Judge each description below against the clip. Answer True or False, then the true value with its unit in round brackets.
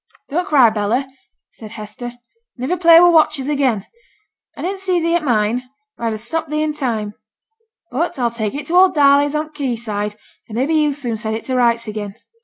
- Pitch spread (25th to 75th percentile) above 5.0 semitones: True (5.6 semitones)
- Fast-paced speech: True (210 wpm)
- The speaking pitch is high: True (265 Hz)